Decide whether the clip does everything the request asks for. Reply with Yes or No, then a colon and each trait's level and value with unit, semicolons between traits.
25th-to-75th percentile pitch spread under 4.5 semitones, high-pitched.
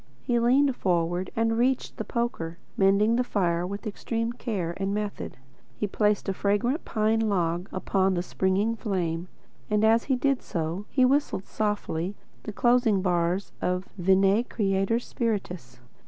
Yes: average, 3.9 semitones; high, 205 Hz